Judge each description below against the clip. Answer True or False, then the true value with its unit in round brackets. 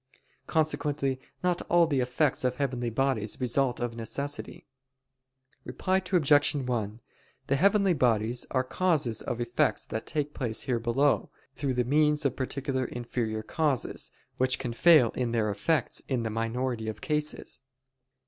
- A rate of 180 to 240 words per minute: False (145 wpm)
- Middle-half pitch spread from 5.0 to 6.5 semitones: False (3.8 semitones)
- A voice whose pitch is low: True (130 Hz)